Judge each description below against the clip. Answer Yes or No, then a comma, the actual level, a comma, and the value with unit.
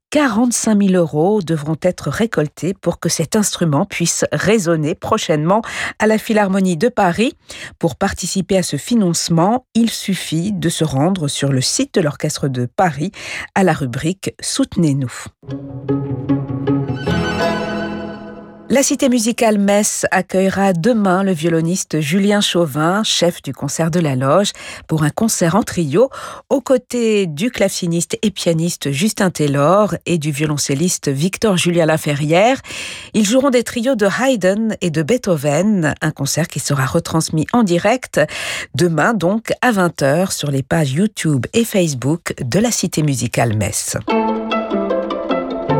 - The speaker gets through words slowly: Yes, slow, 140 wpm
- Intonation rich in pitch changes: Yes, wide, 5.8 semitones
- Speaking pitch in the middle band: Yes, medium, 180 Hz